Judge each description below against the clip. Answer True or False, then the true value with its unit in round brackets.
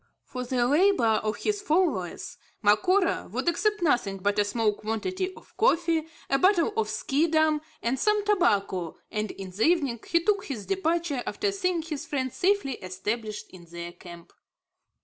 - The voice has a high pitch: True (280 Hz)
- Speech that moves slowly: False (160 wpm)